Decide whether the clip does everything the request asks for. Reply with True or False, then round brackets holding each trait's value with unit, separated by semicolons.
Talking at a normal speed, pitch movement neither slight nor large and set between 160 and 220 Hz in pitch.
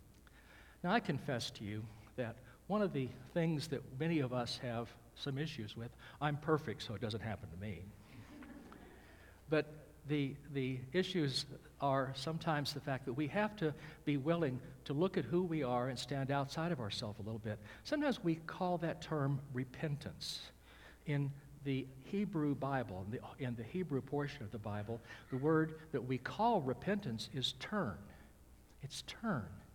False (165 wpm; 5.0 semitones; 135 Hz)